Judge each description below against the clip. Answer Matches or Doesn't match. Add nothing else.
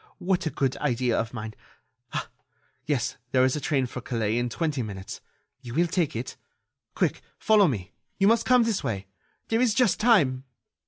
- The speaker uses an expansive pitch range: Matches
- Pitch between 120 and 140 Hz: Matches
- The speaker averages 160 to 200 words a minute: Matches